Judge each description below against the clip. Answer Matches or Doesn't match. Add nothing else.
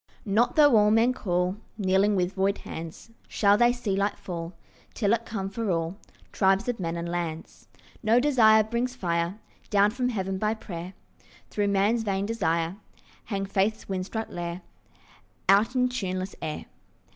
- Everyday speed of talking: Matches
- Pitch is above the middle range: Matches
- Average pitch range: Matches